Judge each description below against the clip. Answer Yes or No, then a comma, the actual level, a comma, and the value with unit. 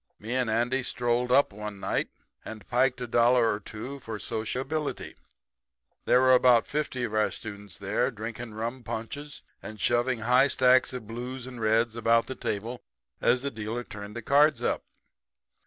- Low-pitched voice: Yes, low, 120 Hz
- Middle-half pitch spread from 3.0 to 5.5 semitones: No, narrow, 2.6 semitones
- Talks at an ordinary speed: Yes, average, 170 wpm